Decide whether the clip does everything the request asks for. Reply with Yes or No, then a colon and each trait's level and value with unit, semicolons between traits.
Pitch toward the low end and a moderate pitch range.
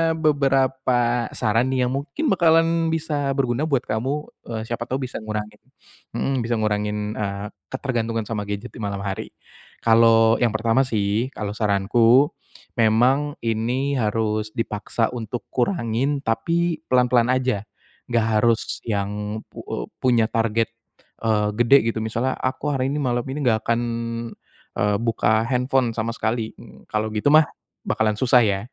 Yes: low, 115 Hz; average, 3.3 semitones